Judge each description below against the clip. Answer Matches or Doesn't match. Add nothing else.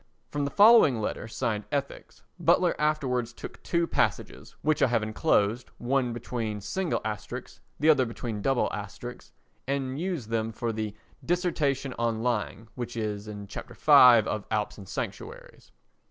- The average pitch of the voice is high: Doesn't match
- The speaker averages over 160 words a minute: Doesn't match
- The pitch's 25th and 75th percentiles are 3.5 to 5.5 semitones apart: Matches